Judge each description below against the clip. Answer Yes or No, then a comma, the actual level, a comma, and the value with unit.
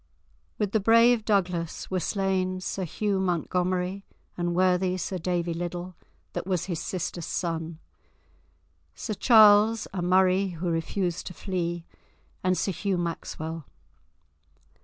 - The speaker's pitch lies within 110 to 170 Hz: No, medium, 185 Hz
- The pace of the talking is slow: Yes, slow, 125 wpm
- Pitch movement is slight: Yes, narrow, 2.0 semitones